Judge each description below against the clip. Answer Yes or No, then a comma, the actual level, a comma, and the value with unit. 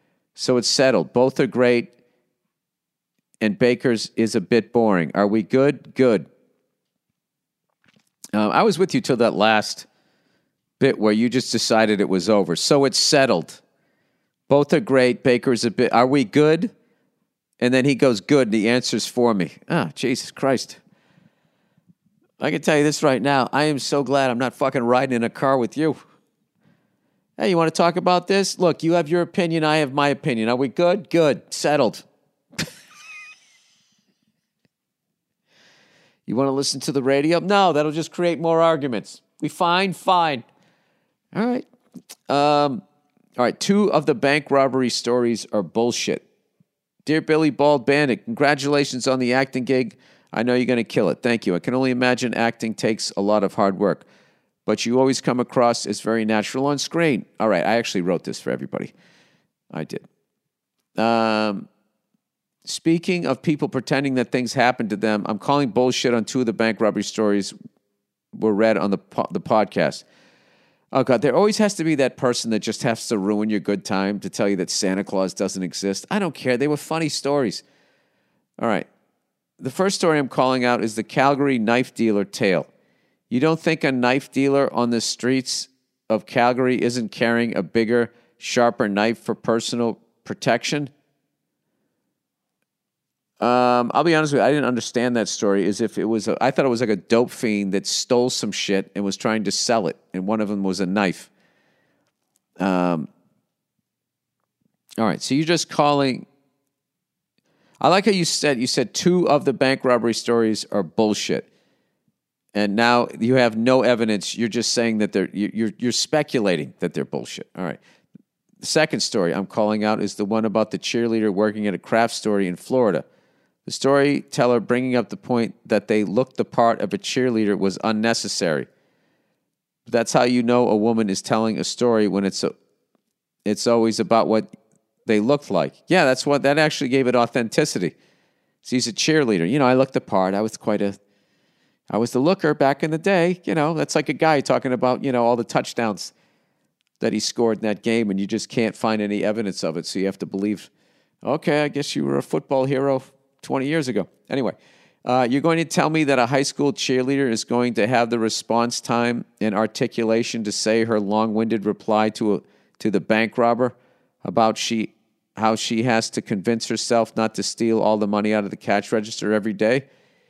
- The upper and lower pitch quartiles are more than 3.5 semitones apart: Yes, average, 4.5 semitones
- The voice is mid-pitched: No, low, 120 Hz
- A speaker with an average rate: Yes, average, 190 wpm